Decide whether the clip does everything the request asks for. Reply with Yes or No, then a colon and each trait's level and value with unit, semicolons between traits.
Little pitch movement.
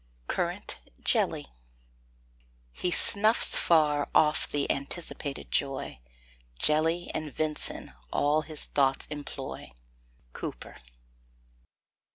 Yes: narrow, 2.1 semitones